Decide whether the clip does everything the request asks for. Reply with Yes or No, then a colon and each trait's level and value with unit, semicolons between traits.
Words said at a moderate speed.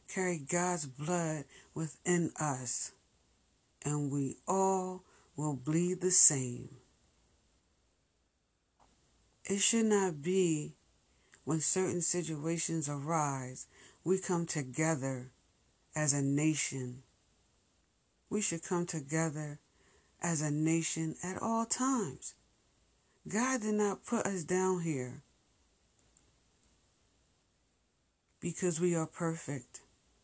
No: slow, 95 wpm